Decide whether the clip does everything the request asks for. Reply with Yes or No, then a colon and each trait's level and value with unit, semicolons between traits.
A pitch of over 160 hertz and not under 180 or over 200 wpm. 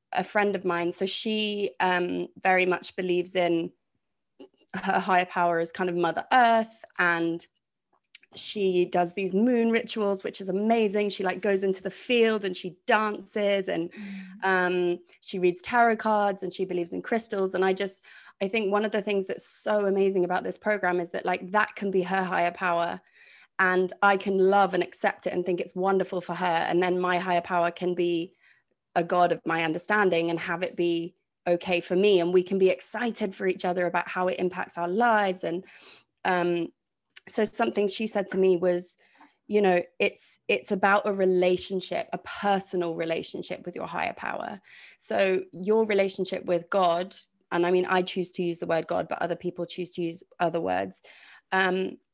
Yes: medium, 185 Hz; average, 190 wpm